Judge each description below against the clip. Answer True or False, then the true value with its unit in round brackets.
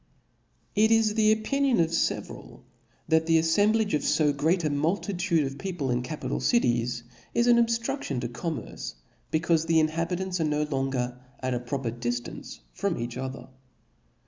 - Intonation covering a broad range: True (6.9 semitones)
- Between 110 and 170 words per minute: True (155 wpm)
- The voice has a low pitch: False (160 Hz)